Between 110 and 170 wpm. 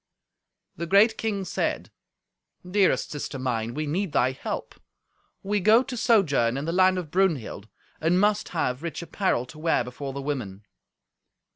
Yes: average, 155 wpm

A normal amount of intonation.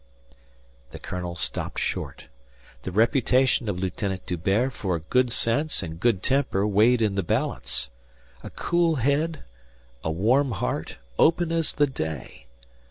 No: wide, 7.0 semitones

